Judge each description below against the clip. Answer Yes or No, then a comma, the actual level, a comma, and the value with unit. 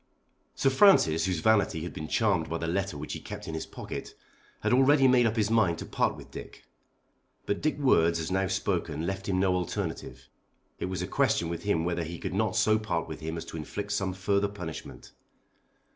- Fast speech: Yes, fast, 210 wpm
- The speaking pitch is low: Yes, very low, 95 Hz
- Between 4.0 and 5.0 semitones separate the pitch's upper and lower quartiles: Yes, average, 4.5 semitones